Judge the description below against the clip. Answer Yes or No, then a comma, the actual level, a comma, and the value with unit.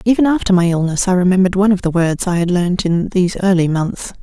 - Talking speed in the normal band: No, fast, 240 wpm